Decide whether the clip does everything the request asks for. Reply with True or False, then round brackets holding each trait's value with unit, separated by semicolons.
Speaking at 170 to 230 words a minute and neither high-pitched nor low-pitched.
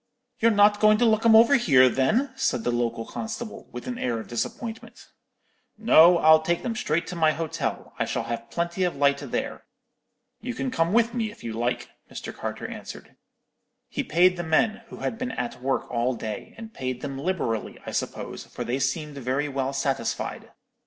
True (195 wpm; 160 Hz)